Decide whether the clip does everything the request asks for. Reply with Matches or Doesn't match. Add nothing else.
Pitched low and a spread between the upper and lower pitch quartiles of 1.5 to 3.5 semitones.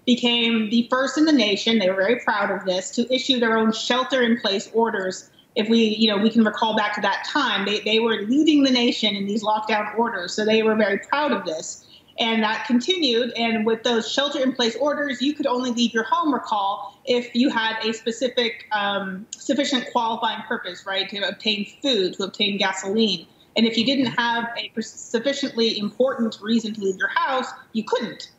Doesn't match